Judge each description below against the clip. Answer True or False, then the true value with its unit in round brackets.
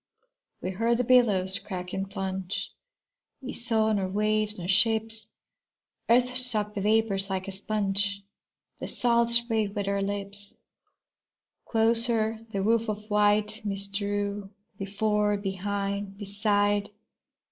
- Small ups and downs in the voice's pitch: True (2.0 semitones)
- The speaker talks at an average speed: False (125 wpm)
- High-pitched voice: True (205 Hz)